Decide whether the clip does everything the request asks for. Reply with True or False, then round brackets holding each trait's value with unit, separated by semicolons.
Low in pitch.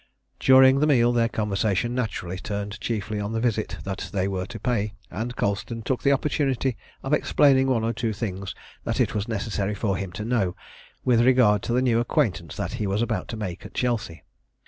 True (110 Hz)